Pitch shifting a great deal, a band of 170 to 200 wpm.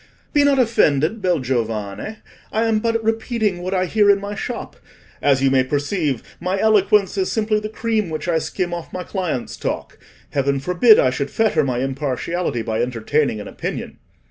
Yes: wide, 7.8 semitones; average, 180 wpm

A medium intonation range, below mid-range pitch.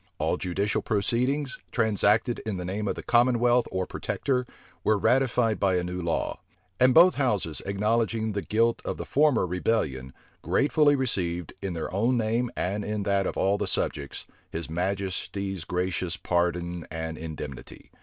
Yes: average, 4.8 semitones; low, 100 Hz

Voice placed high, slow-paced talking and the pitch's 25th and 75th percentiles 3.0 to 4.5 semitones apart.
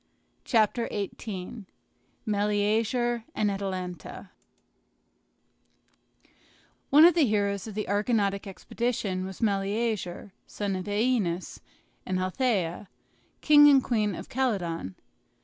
Yes: high, 205 Hz; slow, 95 wpm; average, 3.5 semitones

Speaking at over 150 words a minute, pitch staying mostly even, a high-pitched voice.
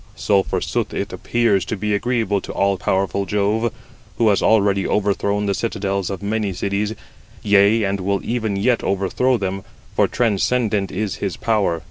No: average, 160 wpm; narrow, 2.0 semitones; low, 100 Hz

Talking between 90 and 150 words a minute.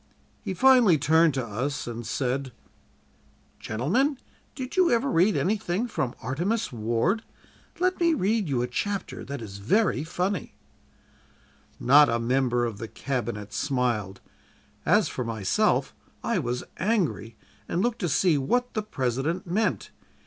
Yes: average, 140 wpm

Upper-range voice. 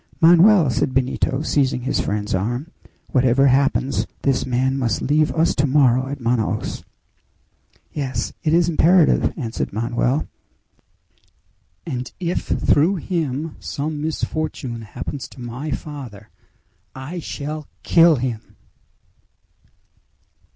No: low, 135 Hz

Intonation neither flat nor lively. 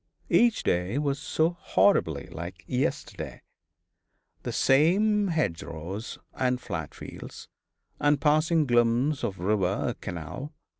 No: wide, 8.7 semitones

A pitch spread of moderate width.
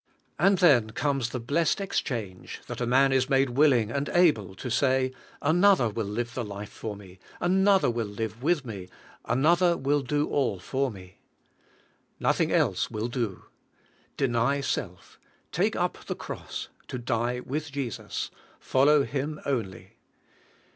Yes: average, 4.2 semitones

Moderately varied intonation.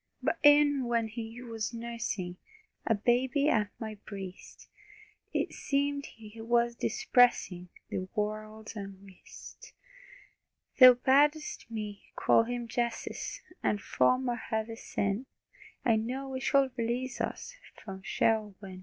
Yes: average, 3.2 semitones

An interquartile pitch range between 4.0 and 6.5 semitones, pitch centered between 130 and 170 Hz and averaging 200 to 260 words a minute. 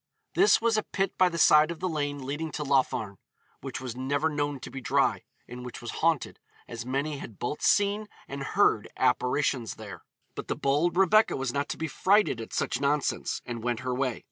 Yes: average, 4.4 semitones; medium, 140 Hz; fast, 205 wpm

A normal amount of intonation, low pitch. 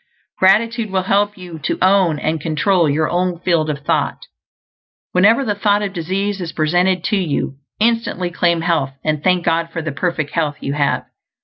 No: average, 3.8 semitones; medium, 175 Hz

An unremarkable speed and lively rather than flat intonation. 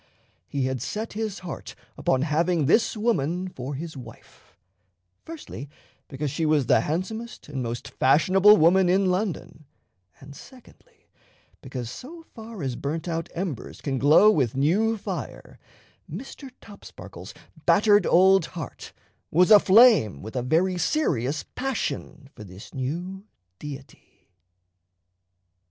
No: slow, 125 wpm; wide, 7.2 semitones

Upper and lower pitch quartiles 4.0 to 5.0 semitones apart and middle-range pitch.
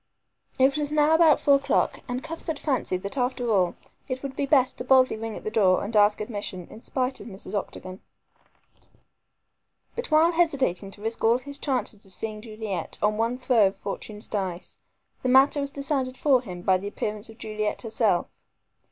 No: average, 4.7 semitones; high, 230 Hz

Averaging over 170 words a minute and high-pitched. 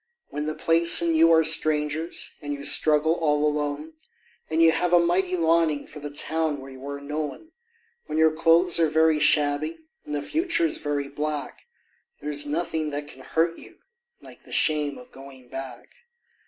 No: average, 180 wpm; medium, 155 Hz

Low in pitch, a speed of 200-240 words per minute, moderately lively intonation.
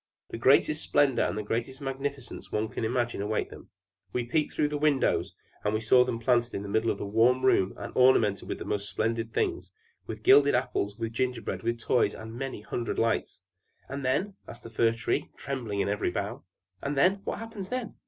Yes: low, 120 Hz; fast, 205 wpm; average, 3.6 semitones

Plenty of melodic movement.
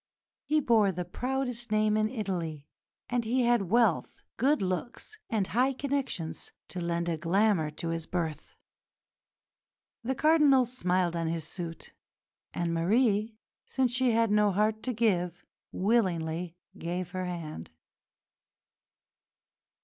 Yes: wide, 5.9 semitones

